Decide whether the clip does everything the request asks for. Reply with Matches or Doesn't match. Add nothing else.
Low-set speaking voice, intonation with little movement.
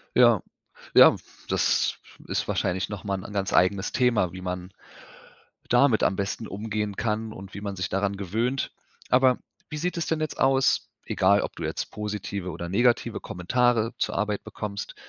Doesn't match